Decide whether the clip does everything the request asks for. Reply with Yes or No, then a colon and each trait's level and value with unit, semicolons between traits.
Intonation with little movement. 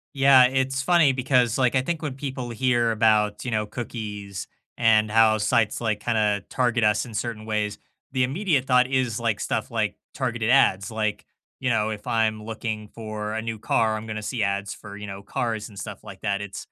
No: average, 3.0 semitones